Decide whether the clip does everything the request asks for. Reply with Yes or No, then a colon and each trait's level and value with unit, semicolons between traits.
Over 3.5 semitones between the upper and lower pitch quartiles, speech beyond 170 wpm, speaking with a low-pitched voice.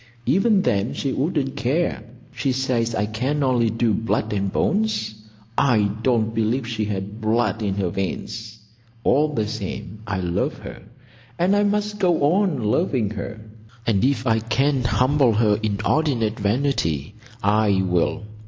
No: average, 4.6 semitones; average, 150 wpm; low, 115 Hz